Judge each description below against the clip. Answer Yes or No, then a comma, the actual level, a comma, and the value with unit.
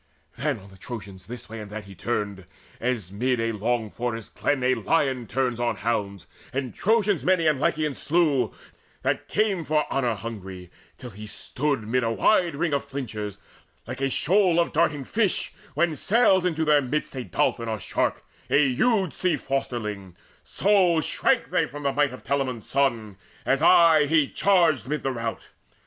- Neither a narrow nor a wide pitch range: No, wide, 5.9 semitones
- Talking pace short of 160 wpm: No, average, 170 wpm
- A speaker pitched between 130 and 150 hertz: Yes, low, 135 Hz